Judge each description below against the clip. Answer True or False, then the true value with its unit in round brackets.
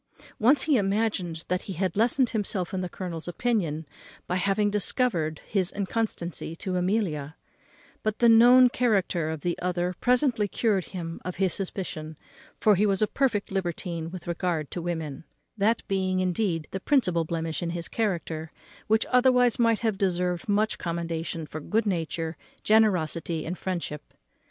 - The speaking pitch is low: False (185 Hz)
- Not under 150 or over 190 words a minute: True (155 wpm)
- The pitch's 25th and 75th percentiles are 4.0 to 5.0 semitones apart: True (4.3 semitones)